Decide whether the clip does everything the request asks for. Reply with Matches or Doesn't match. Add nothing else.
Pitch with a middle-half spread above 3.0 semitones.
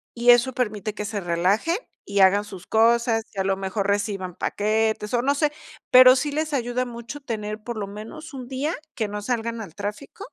Matches